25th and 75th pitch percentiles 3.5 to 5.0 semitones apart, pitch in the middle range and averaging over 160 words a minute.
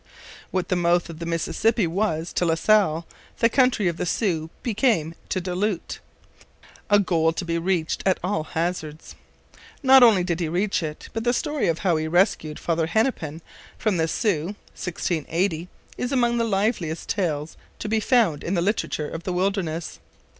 Yes: average, 4.4 semitones; medium, 180 Hz; average, 175 wpm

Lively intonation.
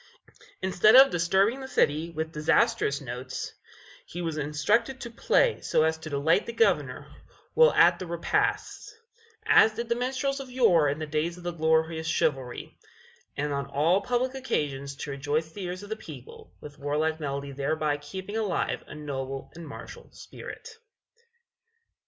Yes: wide, 6.7 semitones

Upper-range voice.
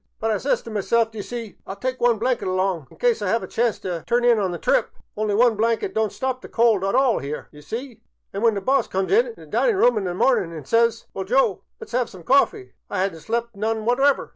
Yes: high, 225 Hz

